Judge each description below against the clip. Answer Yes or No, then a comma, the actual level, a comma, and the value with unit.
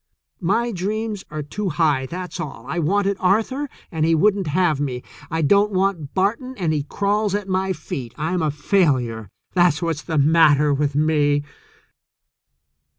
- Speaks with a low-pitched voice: No, medium, 165 Hz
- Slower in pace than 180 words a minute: Yes, average, 155 wpm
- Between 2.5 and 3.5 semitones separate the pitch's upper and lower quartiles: No, average, 5.0 semitones